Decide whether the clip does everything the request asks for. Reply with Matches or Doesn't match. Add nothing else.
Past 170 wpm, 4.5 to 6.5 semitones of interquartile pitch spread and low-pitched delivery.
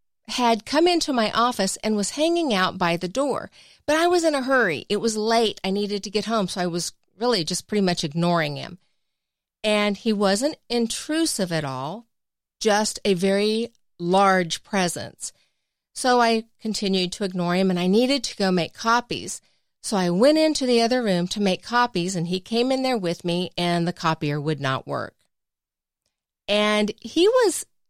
Doesn't match